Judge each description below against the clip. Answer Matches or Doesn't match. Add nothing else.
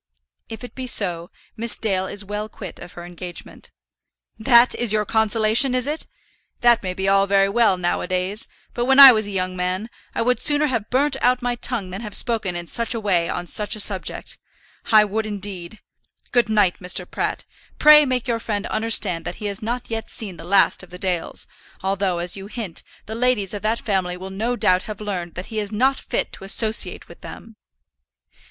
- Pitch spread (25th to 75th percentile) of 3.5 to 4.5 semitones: Matches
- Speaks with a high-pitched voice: Matches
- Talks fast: Matches